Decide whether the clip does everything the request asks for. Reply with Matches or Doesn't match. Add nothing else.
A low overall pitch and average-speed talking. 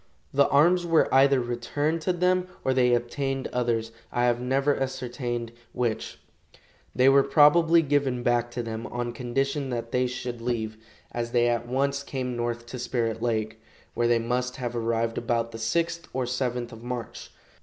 Matches